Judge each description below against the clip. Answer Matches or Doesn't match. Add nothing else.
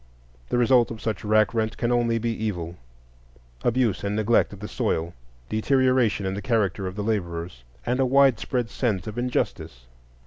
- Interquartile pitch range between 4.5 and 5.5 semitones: Matches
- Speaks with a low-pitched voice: Matches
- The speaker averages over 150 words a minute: Matches